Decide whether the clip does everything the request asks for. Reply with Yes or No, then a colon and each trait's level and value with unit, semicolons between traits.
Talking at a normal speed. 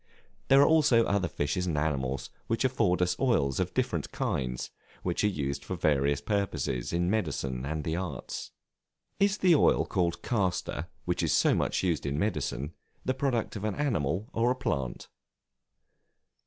Yes: average, 165 wpm